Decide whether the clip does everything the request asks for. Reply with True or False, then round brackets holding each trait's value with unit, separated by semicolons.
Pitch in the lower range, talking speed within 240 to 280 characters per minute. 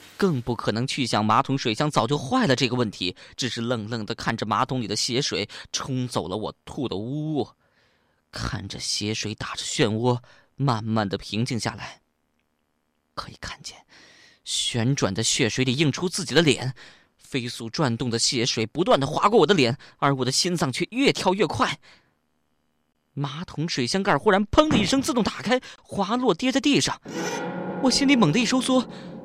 True (130 Hz; 250 characters per minute)